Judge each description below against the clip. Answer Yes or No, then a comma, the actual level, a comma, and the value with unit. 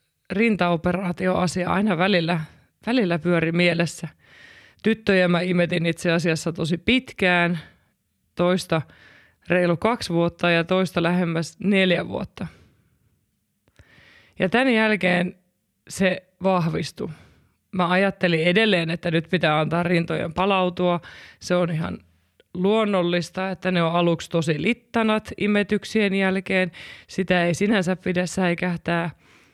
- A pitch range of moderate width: No, narrow, 1.9 semitones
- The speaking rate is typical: Yes, average, 110 wpm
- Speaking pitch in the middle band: Yes, medium, 180 Hz